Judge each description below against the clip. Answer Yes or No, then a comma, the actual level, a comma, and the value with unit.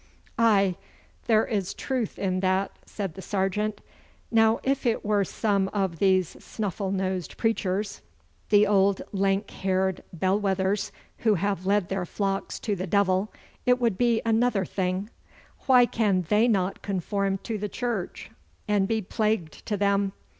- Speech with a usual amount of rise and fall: No, narrow, 2.3 semitones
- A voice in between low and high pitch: No, high, 200 Hz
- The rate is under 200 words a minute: Yes, average, 150 wpm